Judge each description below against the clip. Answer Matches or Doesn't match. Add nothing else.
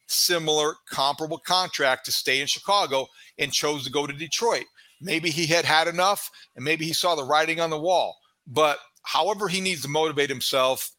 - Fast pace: Doesn't match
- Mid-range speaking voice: Matches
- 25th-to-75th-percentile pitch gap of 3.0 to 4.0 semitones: Matches